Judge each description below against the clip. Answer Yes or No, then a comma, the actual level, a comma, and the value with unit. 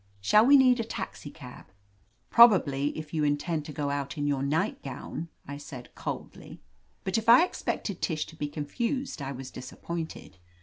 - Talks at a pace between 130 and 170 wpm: Yes, average, 165 wpm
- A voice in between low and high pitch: Yes, medium, 150 Hz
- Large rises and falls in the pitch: Yes, wide, 6.3 semitones